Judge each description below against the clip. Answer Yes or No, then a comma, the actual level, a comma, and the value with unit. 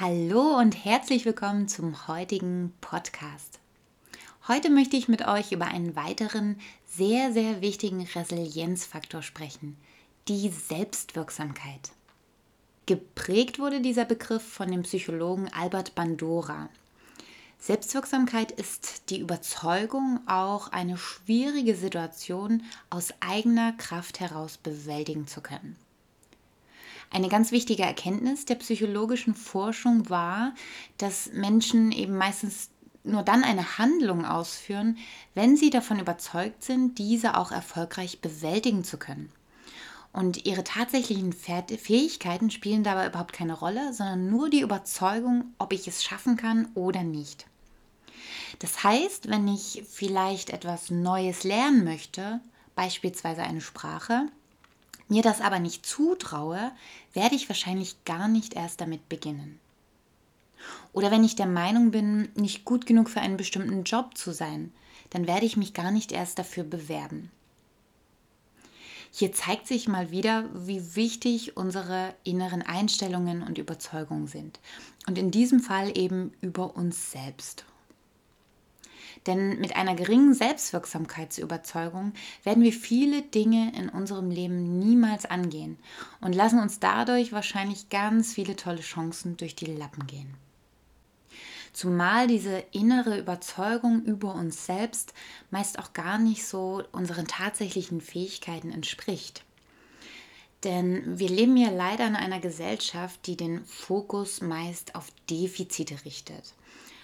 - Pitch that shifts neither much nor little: Yes, average, 4.4 semitones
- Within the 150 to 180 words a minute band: No, slow, 125 wpm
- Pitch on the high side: Yes, high, 195 Hz